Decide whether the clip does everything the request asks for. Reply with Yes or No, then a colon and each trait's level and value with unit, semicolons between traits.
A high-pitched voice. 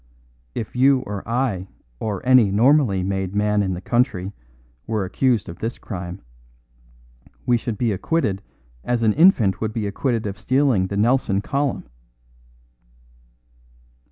No: low, 110 Hz